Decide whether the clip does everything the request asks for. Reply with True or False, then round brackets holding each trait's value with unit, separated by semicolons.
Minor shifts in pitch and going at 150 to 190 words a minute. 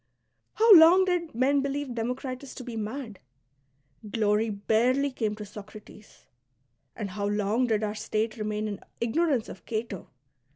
False (4.4 semitones; 155 wpm)